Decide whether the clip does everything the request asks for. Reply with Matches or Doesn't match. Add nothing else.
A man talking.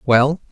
Matches